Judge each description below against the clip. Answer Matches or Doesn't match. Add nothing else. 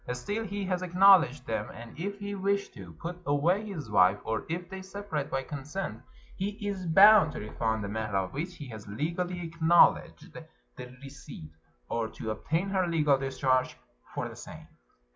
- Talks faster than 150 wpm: Matches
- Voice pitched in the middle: Matches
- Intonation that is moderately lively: Doesn't match